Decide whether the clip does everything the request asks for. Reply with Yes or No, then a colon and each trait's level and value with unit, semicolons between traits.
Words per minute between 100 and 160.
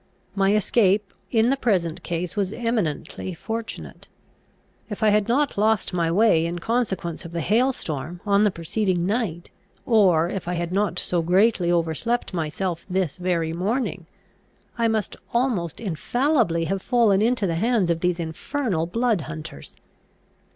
Yes: average, 150 wpm